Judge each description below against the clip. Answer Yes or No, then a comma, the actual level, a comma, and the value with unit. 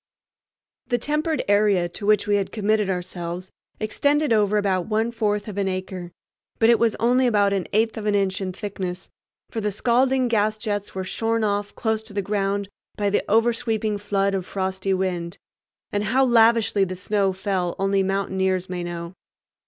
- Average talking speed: Yes, average, 175 wpm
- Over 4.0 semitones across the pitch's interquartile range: No, average, 2.7 semitones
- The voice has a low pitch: No, high, 205 Hz